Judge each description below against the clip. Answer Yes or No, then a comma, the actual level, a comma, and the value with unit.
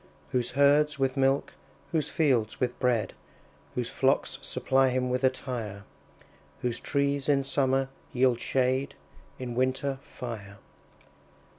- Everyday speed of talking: No, slow, 120 wpm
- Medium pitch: No, low, 130 Hz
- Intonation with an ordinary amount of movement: No, narrow, 1.9 semitones